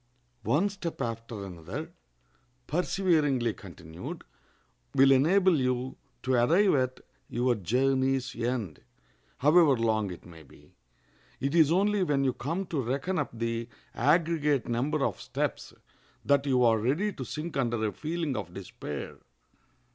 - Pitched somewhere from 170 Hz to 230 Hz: No, low, 135 Hz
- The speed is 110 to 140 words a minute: Yes, slow, 135 wpm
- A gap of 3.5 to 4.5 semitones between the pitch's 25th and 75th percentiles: No, average, 5.1 semitones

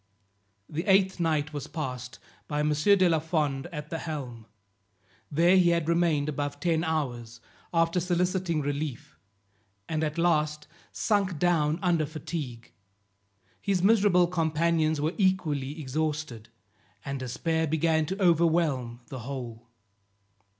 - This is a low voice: No, medium, 155 Hz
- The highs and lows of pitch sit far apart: No, average, 3.1 semitones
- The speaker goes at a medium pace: No, slow, 125 wpm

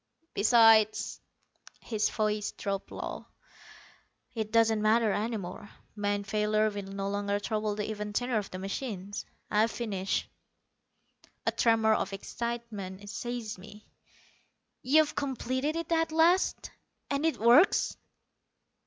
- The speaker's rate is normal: No, slow, 120 wpm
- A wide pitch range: No, narrow, 2.6 semitones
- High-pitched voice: Yes, high, 215 Hz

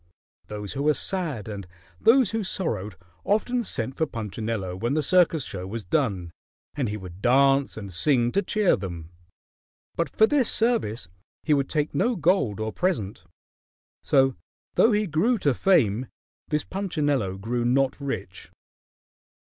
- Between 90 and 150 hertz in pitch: Yes, low, 135 Hz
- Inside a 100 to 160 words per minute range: Yes, average, 150 wpm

